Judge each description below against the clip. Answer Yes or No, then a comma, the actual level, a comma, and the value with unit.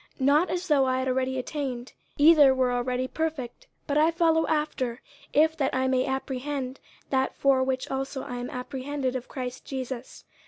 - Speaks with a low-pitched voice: No, very high, 265 Hz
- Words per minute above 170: Yes, average, 180 wpm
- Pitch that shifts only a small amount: Yes, narrow, 2.3 semitones